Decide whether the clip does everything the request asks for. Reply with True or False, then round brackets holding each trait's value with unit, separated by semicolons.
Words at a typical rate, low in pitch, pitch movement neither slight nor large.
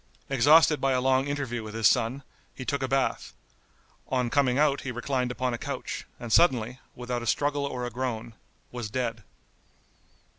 False (175 wpm; 130 Hz; 2.2 semitones)